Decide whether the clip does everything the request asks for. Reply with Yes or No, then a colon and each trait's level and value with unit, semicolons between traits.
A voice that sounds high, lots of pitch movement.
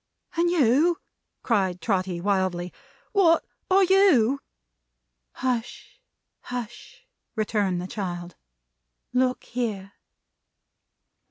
Yes: high, 225 Hz; wide, 7.5 semitones